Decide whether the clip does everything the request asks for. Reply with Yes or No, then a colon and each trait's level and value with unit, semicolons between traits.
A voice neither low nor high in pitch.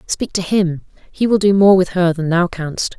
Yes: medium, 180 Hz